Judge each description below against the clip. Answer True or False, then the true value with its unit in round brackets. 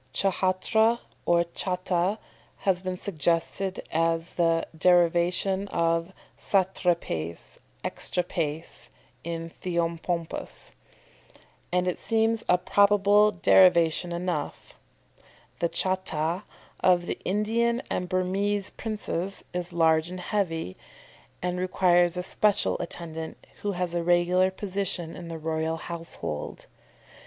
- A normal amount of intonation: False (2.3 semitones)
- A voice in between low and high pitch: True (180 Hz)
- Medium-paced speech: False (105 wpm)